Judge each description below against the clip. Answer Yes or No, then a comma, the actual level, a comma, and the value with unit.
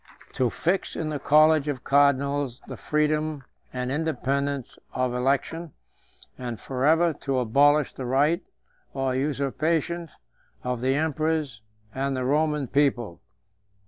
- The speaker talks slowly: Yes, slow, 120 wpm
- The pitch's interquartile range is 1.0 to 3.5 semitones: Yes, average, 2.9 semitones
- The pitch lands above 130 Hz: Yes, medium, 140 Hz